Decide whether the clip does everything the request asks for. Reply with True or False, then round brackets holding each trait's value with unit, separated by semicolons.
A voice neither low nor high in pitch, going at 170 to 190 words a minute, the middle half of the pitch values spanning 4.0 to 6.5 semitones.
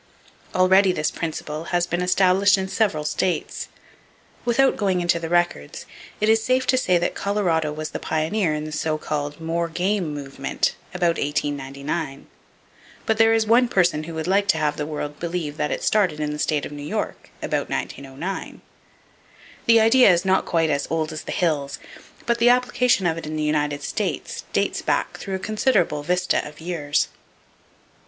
True (170 Hz; 180 wpm; 4.4 semitones)